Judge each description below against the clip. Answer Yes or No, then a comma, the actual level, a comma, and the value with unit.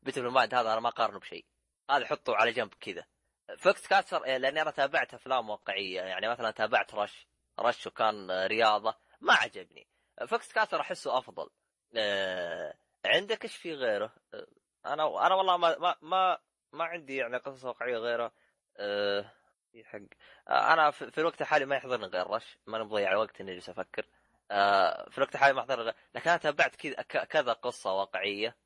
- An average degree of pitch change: No, wide, 6.8 semitones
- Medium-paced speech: No, fast, 165 wpm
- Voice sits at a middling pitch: No, low, 125 Hz